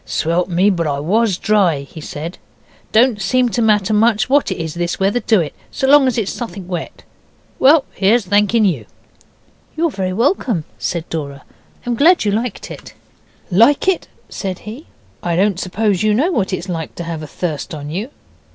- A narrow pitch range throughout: No, average, 5.3 semitones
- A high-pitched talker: Yes, high, 200 Hz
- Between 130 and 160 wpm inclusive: No, average, 190 wpm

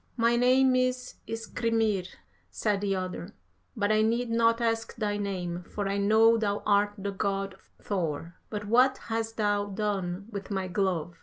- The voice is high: Yes, high, 205 Hz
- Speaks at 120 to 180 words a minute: Yes, average, 160 wpm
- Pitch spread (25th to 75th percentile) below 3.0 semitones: Yes, narrow, 2.6 semitones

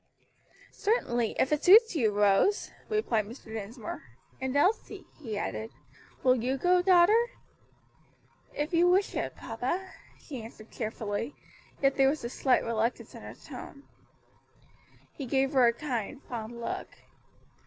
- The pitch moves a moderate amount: No, wide, 6.9 semitones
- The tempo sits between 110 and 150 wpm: Yes, average, 140 wpm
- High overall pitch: Yes, very high, 260 Hz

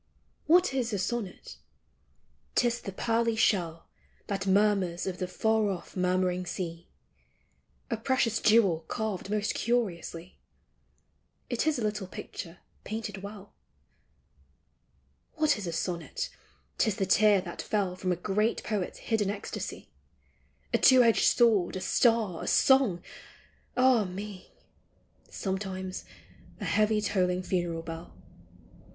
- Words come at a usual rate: No, slow, 130 wpm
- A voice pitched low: No, high, 200 Hz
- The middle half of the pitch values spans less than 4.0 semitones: Yes, average, 3.5 semitones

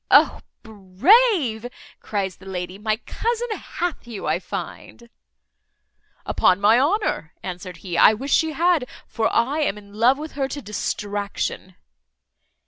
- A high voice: Yes, high, 220 Hz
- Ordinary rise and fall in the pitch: No, wide, 6.9 semitones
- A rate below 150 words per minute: Yes, slow, 135 wpm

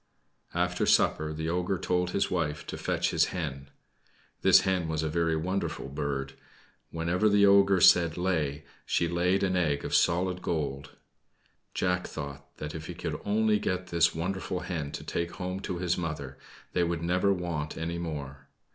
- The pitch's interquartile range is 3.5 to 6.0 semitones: No, average, 3.0 semitones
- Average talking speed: Yes, average, 170 wpm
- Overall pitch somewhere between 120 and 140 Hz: No, very low, 85 Hz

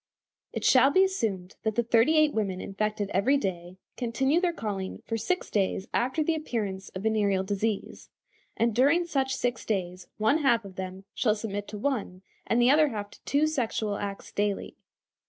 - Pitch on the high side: Yes, high, 220 Hz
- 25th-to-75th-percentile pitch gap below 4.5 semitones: No, average, 5.3 semitones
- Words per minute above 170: Yes, average, 180 wpm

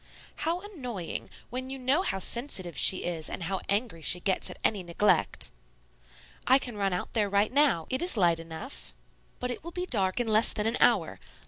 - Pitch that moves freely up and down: Yes, wide, 5.9 semitones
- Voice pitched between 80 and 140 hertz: No, high, 215 Hz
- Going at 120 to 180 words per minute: No, average, 195 wpm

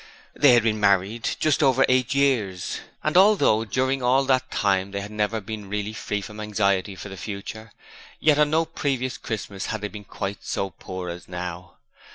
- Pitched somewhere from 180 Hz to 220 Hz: No, low, 105 Hz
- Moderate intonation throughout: Yes, average, 4.8 semitones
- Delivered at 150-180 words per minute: No, average, 190 wpm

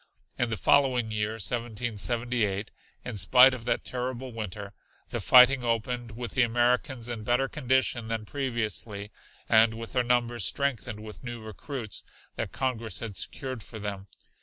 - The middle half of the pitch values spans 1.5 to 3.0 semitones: Yes, narrow, 2.4 semitones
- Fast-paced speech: No, average, 150 wpm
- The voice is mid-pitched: No, low, 120 Hz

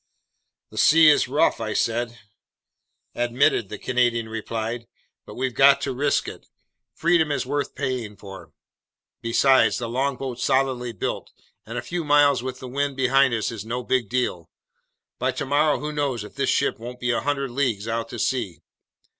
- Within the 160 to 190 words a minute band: Yes, average, 165 wpm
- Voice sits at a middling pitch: No, low, 125 Hz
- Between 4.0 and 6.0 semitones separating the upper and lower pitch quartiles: No, average, 3.3 semitones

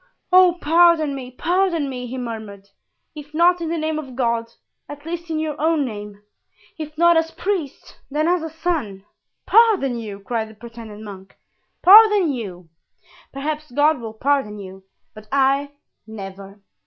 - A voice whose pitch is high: Yes, very high, 275 Hz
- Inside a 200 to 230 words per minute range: No, average, 155 wpm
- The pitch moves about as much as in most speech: No, wide, 6.8 semitones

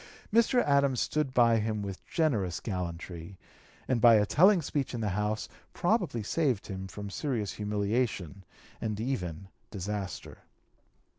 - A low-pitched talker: Yes, low, 105 Hz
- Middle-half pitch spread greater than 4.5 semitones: Yes, average, 4.9 semitones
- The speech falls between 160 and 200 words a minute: No, slow, 135 wpm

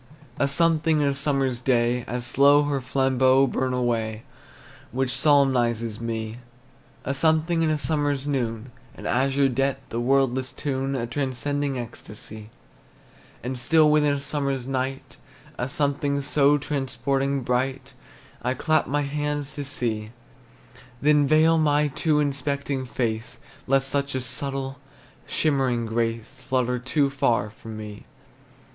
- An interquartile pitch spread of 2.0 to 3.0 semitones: Yes, average, 2.7 semitones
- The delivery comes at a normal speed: No, slow, 130 wpm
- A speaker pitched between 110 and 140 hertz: Yes, low, 135 Hz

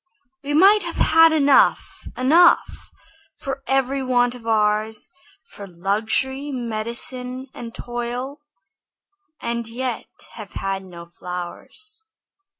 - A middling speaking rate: No, slow, 105 wpm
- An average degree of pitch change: Yes, average, 4.3 semitones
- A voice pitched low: No, high, 245 Hz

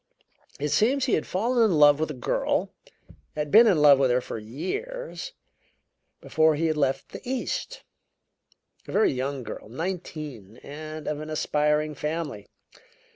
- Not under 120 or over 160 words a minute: Yes, average, 155 wpm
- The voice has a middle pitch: Yes, medium, 155 Hz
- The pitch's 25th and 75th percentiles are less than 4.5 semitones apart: No, average, 4.9 semitones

